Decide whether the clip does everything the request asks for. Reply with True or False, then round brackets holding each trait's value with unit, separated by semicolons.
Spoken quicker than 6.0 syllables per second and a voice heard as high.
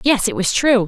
False (5.2 syllables/s; 220 Hz)